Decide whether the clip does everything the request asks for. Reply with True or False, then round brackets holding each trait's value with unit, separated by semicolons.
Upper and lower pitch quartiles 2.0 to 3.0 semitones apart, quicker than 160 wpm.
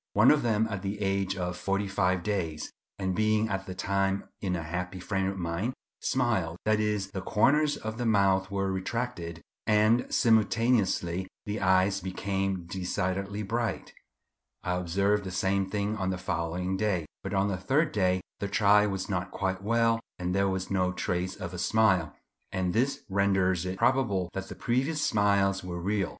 True (2.4 semitones; 175 wpm)